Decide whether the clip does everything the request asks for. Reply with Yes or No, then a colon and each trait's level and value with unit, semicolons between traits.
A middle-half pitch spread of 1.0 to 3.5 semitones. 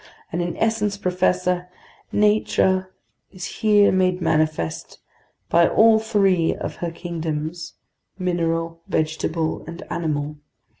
Yes: narrow, 2.5 semitones